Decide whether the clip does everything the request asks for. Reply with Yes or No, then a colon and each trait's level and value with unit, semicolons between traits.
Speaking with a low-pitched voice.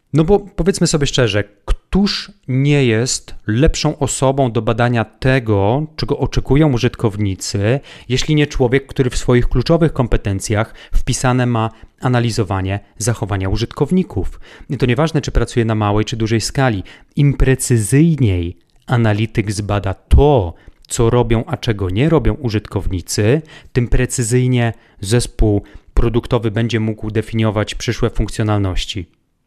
Yes: low, 120 Hz